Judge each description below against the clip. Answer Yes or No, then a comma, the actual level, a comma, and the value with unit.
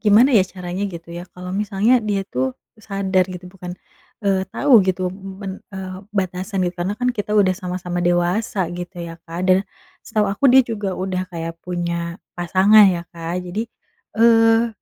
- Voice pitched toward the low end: No, high, 190 Hz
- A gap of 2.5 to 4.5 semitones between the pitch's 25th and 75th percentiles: Yes, average, 2.8 semitones